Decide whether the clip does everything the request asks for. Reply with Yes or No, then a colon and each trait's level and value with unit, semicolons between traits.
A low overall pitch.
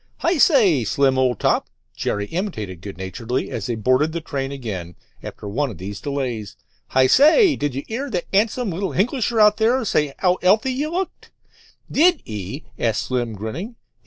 No: medium, 145 Hz